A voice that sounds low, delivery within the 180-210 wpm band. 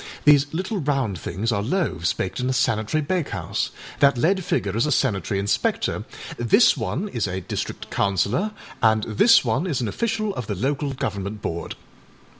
No: low, 125 Hz; average, 170 wpm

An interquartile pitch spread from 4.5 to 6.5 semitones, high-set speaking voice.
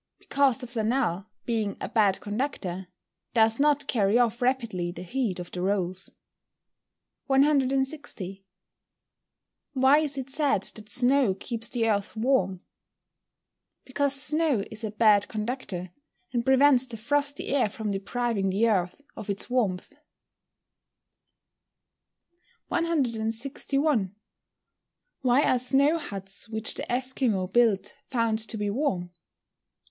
Yes: average, 4.9 semitones; high, 230 Hz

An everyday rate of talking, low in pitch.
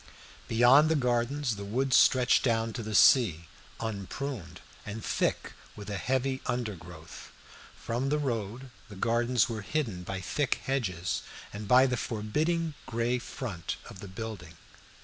Yes: average, 145 wpm; low, 115 Hz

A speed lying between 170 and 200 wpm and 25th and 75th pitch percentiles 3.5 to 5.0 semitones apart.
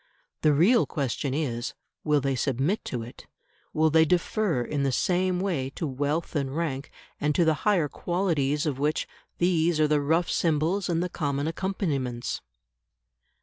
No: average, 160 wpm; average, 3.8 semitones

